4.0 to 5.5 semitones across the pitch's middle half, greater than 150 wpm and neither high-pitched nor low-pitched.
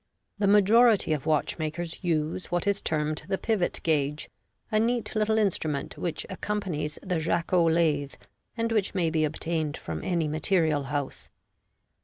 No: average, 4.6 semitones; average, 145 wpm; medium, 165 Hz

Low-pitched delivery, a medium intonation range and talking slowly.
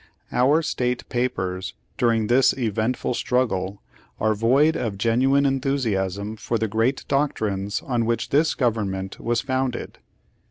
Yes: low, 120 Hz; average, 3.9 semitones; slow, 125 wpm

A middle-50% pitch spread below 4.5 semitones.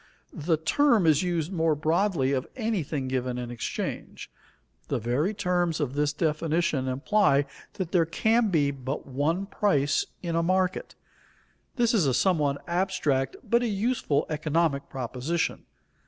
No: average, 5.0 semitones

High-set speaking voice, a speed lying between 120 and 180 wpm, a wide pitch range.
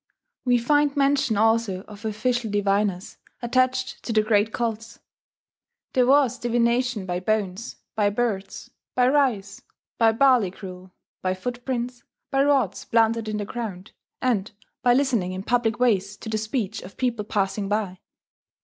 No: high, 225 Hz; average, 145 wpm; average, 3.4 semitones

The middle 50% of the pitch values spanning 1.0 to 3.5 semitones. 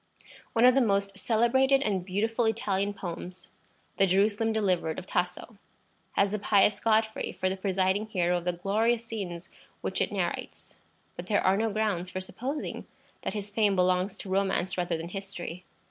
Yes: average, 3.0 semitones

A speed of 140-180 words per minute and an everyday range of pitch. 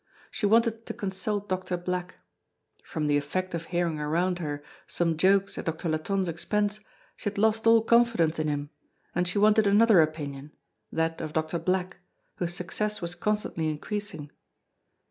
Yes: average, 160 wpm; average, 4.5 semitones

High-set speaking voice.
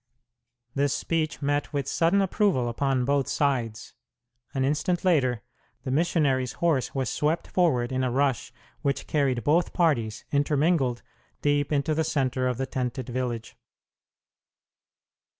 No: medium, 140 Hz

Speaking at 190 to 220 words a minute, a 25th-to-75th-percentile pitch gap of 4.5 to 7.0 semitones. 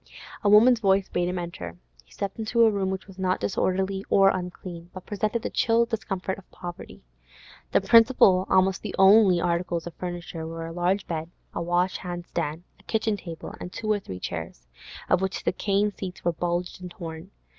No: average, 195 wpm; narrow, 2.5 semitones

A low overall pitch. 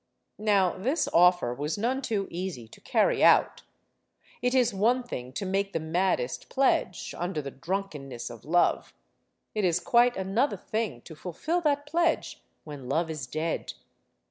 No: medium, 185 Hz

